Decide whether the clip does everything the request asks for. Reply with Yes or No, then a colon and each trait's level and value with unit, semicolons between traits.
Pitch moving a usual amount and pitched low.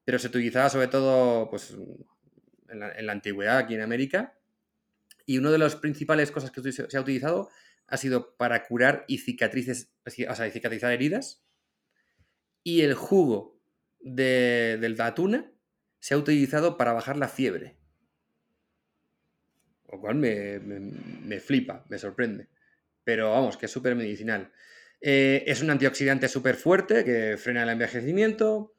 Yes: average, 4.2 semitones; low, 130 Hz